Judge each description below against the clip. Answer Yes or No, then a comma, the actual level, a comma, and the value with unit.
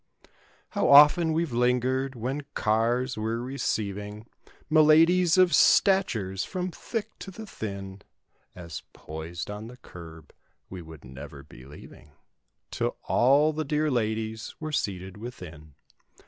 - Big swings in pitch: Yes, wide, 8.1 semitones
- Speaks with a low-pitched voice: Yes, low, 115 Hz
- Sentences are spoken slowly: Yes, slow, 125 wpm